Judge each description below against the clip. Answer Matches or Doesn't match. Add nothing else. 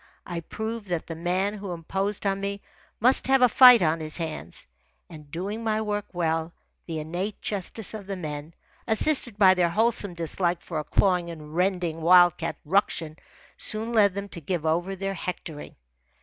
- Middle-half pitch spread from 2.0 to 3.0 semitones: Doesn't match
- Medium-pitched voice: Matches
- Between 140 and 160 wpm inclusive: Doesn't match